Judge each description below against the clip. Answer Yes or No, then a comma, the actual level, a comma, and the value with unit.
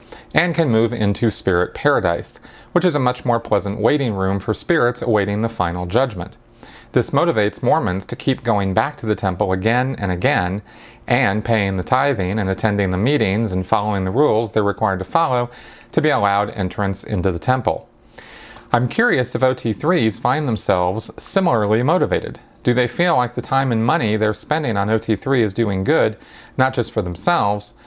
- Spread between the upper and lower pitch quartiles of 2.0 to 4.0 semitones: Yes, average, 3.6 semitones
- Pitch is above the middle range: No, low, 110 Hz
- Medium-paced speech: Yes, average, 180 wpm